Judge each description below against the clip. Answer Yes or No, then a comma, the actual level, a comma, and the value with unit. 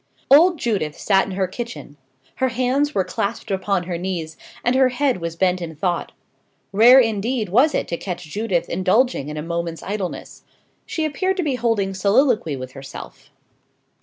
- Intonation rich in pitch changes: Yes, wide, 6.3 semitones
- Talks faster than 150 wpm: Yes, average, 170 wpm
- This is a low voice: No, high, 200 Hz